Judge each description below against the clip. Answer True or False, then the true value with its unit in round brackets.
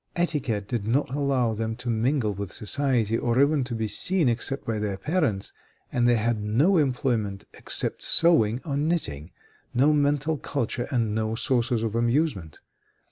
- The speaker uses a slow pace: False (160 wpm)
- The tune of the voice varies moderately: True (4.5 semitones)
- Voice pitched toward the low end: True (120 Hz)